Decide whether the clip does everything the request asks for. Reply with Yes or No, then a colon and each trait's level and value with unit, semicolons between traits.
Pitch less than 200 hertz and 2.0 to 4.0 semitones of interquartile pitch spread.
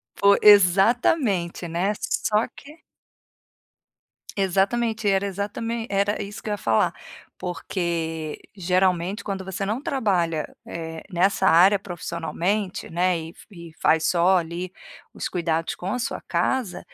Yes: high, 190 Hz; average, 3.3 semitones